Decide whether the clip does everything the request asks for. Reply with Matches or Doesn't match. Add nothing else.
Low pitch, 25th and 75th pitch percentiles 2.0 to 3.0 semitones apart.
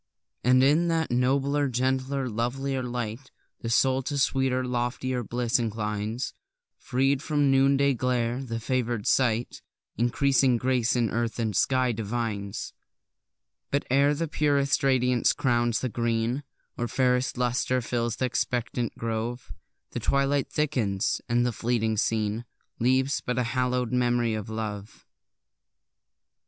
Matches